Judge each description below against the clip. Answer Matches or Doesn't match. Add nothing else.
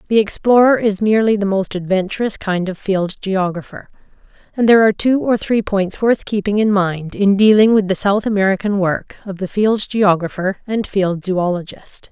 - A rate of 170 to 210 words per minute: Matches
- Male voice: Doesn't match